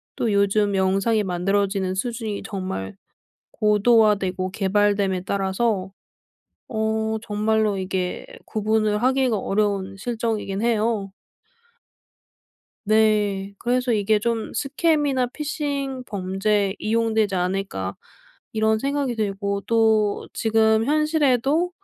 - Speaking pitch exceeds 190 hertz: Yes, high, 215 Hz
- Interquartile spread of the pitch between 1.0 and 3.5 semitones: Yes, average, 2.9 semitones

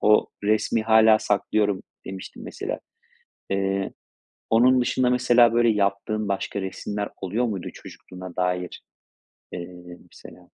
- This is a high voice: No, low, 105 Hz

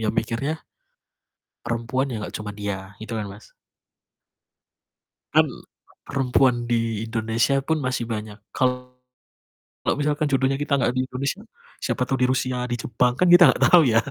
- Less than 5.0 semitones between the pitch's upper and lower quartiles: Yes, average, 3.2 semitones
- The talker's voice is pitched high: No, low, 125 Hz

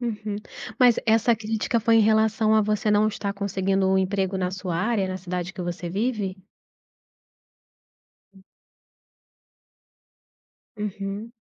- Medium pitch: No, high, 205 Hz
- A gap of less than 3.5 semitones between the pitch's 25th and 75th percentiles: Yes, narrow, 2.4 semitones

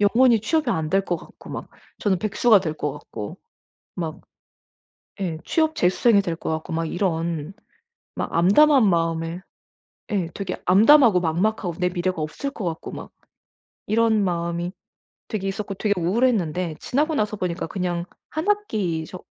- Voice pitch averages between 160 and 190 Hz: Yes, medium, 185 Hz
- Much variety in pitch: No, average, 4.4 semitones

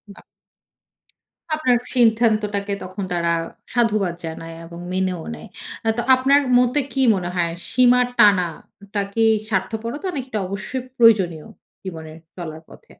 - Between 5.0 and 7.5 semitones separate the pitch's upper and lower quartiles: Yes, wide, 5.4 semitones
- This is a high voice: Yes, high, 200 Hz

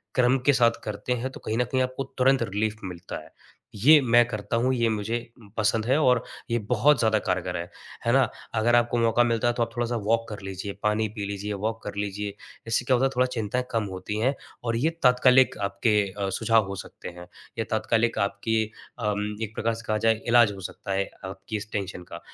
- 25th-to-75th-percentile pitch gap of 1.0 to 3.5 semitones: Yes, average, 2.8 semitones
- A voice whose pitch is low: Yes, low, 115 Hz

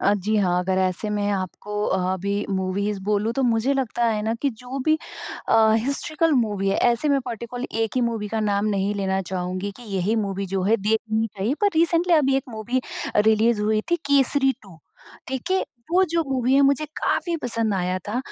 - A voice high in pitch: Yes, high, 220 Hz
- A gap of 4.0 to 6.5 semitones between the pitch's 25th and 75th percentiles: Yes, average, 4.8 semitones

